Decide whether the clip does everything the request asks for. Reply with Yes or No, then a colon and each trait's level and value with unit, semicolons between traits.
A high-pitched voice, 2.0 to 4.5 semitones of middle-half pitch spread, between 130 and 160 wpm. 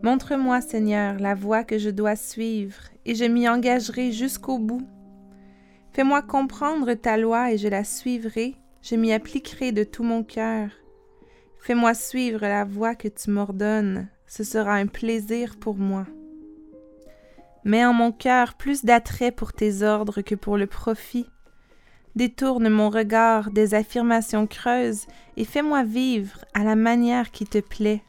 Yes: high, 225 Hz; average, 2.7 semitones; average, 150 wpm